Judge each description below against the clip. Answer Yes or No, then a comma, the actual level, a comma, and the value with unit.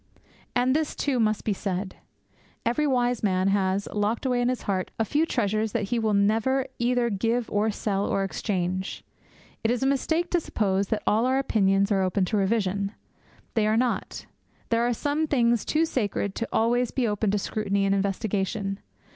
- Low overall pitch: No, high, 220 Hz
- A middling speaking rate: Yes, average, 185 wpm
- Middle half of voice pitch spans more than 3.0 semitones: Yes, average, 3.6 semitones